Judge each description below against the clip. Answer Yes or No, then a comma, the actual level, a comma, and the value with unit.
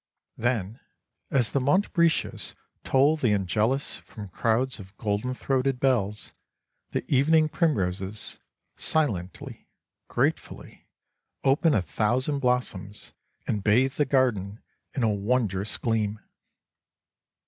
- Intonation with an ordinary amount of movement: Yes, average, 4.6 semitones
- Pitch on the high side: No, low, 120 Hz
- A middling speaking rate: No, slow, 105 wpm